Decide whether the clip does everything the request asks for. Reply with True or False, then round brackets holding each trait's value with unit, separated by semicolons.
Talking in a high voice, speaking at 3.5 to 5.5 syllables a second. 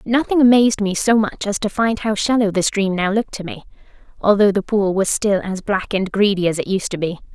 False (205 Hz; 5.7 syllables/s)